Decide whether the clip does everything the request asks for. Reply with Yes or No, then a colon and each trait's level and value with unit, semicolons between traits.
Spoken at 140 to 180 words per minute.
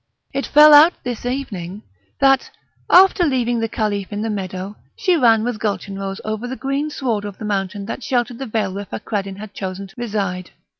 No: average, 190 wpm